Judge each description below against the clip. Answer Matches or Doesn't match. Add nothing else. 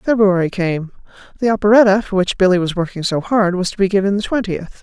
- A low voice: Doesn't match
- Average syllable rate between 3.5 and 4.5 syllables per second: Doesn't match